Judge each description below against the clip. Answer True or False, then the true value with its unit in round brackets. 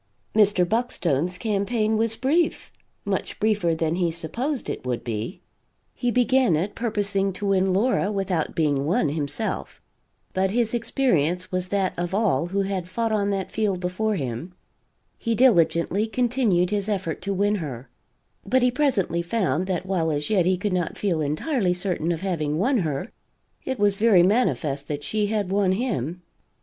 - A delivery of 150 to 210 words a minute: True (165 wpm)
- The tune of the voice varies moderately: True (4.3 semitones)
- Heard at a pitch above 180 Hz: True (190 Hz)